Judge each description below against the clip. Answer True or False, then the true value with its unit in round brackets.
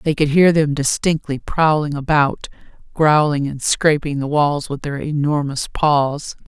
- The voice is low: False (145 Hz)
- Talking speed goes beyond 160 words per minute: False (150 wpm)